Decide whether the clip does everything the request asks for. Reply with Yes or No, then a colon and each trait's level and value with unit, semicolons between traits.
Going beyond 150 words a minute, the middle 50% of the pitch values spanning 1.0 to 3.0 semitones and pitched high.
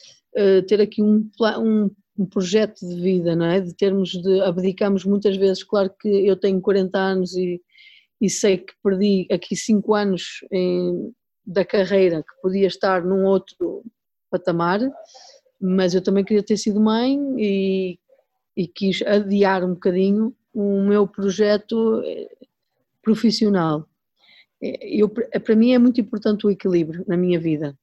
No: average, 140 wpm; narrow, 2.4 semitones; high, 200 Hz